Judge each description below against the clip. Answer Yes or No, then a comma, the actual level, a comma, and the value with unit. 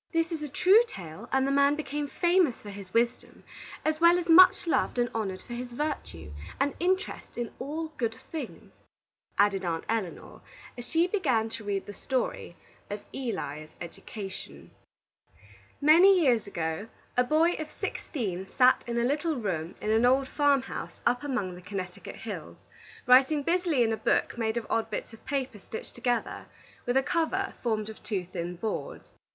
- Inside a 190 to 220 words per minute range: No, average, 175 wpm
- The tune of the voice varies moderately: No, wide, 6.8 semitones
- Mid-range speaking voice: No, high, 245 Hz